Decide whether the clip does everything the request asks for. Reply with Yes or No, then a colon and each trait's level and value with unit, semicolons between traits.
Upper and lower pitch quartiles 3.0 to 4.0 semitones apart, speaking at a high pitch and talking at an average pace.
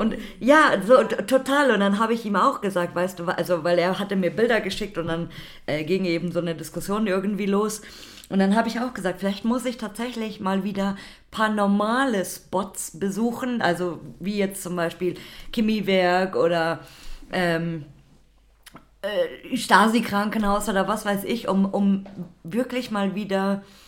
Yes: average, 3.5 semitones; high, 195 Hz; average, 165 wpm